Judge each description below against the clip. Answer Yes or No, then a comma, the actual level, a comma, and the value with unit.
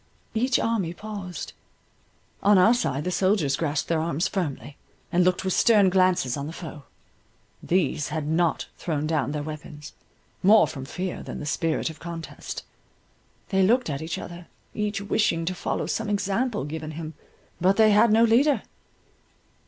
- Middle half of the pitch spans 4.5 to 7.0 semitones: Yes, average, 4.8 semitones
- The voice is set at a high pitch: No, medium, 175 Hz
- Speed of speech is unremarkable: Yes, average, 160 wpm